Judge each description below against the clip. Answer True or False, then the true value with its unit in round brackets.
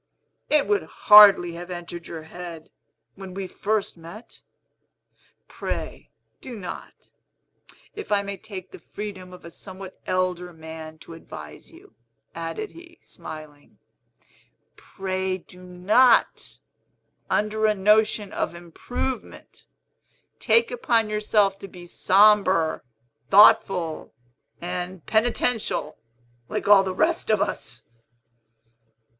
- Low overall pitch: False (190 Hz)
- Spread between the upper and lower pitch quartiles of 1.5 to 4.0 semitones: True (3.5 semitones)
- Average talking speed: False (110 wpm)